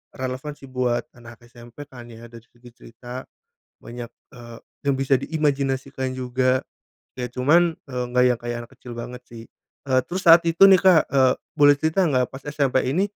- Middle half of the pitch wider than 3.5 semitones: No, average, 3.0 semitones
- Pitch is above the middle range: No, low, 130 Hz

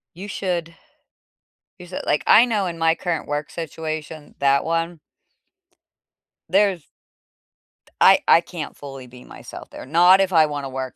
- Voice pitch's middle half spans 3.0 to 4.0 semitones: Yes, average, 3.5 semitones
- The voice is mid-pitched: Yes, medium, 165 Hz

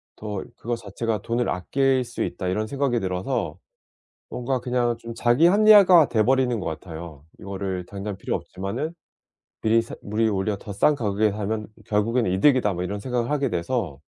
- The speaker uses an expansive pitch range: No, average, 4.3 semitones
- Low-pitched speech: Yes, low, 110 Hz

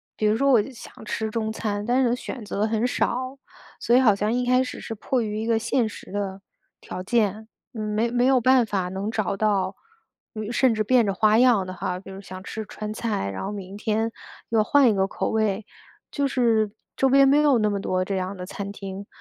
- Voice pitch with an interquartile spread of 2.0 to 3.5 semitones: Yes, average, 3.2 semitones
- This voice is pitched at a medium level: No, high, 215 Hz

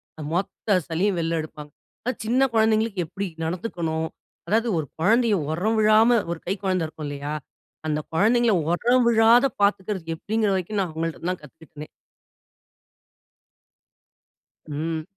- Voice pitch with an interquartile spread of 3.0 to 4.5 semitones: No, wide, 5.4 semitones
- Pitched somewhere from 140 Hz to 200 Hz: Yes, high, 190 Hz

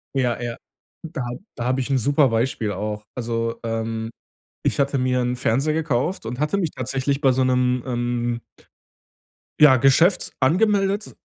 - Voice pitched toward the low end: Yes, low, 125 Hz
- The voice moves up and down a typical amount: Yes, average, 3.1 semitones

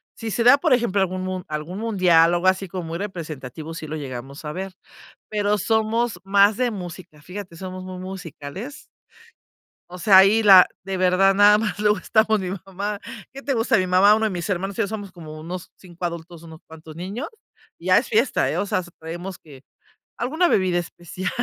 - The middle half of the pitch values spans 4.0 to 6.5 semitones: No, average, 3.4 semitones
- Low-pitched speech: No, medium, 185 Hz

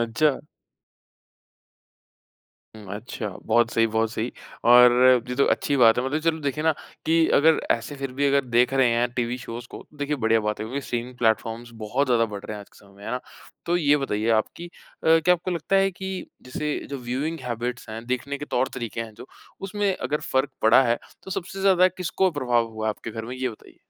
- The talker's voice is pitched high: No, low, 125 Hz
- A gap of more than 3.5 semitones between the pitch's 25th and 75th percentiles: Yes, average, 4.7 semitones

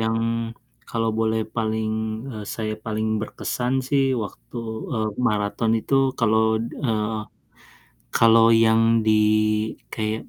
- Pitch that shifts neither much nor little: No, narrow, 1.0 semitones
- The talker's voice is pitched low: Yes, low, 110 Hz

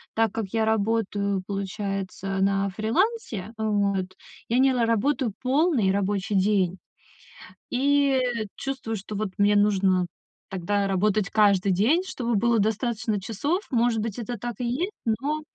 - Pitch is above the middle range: Yes, high, 215 Hz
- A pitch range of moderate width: Yes, average, 3.5 semitones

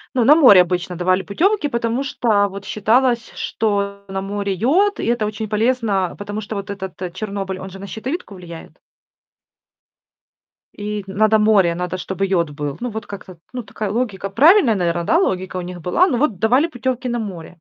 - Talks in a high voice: Yes, high, 205 Hz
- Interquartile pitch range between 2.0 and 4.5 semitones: Yes, average, 4.0 semitones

